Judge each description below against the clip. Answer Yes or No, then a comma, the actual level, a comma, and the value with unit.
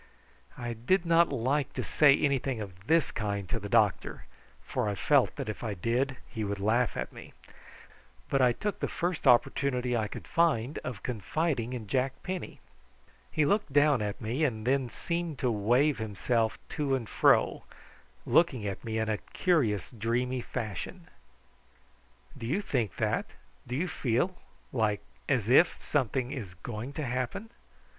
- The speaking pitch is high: No, low, 125 Hz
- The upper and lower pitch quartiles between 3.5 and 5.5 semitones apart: Yes, average, 4.7 semitones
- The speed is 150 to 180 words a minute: Yes, average, 165 wpm